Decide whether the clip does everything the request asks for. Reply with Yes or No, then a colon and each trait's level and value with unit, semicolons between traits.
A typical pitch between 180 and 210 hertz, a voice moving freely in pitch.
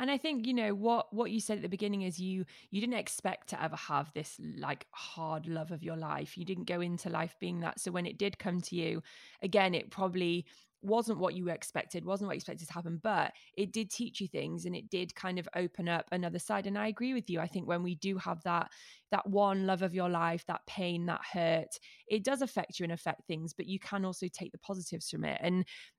No: medium, 185 Hz; average, 2.9 semitones